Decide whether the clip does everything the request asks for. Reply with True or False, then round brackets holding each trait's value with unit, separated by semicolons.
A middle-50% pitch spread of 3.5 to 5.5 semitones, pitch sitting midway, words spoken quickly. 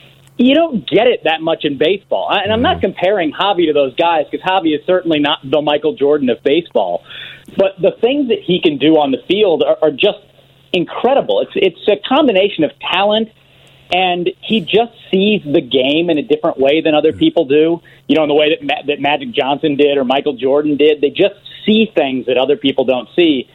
True (5.2 semitones; 160 Hz; 215 wpm)